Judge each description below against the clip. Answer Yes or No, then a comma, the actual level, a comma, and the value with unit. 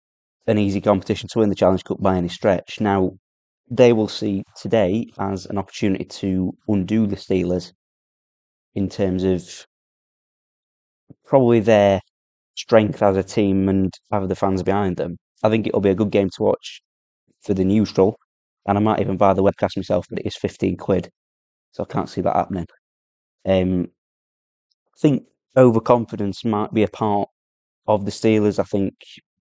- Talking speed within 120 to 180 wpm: Yes, average, 165 wpm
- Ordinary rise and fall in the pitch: No, narrow, 2.3 semitones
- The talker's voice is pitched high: No, low, 100 Hz